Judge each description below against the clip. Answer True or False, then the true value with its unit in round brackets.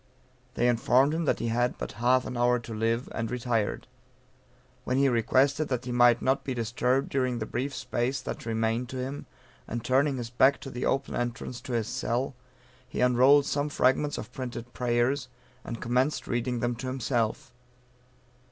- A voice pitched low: True (125 Hz)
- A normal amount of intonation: False (1.9 semitones)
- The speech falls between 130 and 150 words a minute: False (180 wpm)